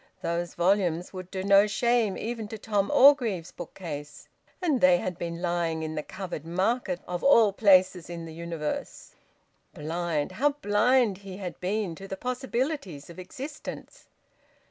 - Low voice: No, medium, 185 Hz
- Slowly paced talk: No, average, 150 wpm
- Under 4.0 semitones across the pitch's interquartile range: No, average, 4.6 semitones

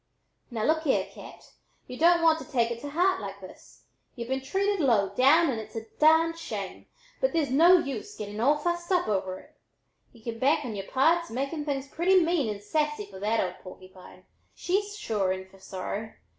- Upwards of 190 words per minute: Yes, average, 200 wpm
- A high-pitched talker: Yes, very high, 270 Hz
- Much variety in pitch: Yes, wide, 7.7 semitones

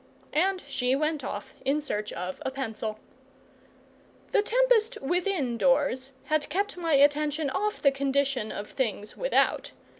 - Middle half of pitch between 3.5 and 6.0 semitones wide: Yes, average, 5.2 semitones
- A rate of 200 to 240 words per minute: No, average, 140 wpm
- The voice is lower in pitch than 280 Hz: No, very high, 285 Hz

